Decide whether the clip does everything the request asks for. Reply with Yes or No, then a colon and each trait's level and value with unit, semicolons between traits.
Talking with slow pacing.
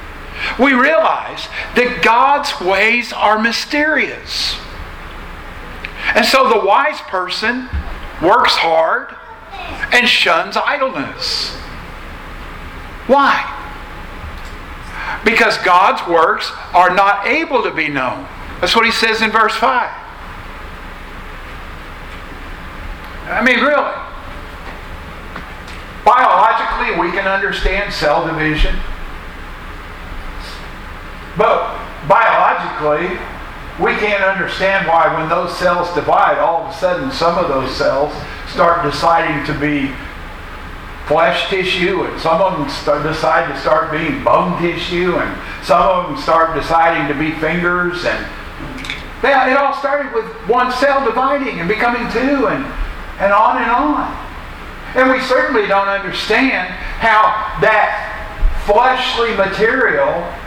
Yes: slow, 110 wpm